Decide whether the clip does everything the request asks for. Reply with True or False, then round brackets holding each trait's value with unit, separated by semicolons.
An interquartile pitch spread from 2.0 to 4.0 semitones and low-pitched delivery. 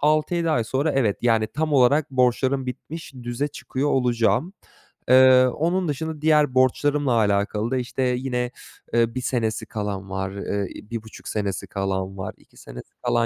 False (4.7 semitones; 125 Hz)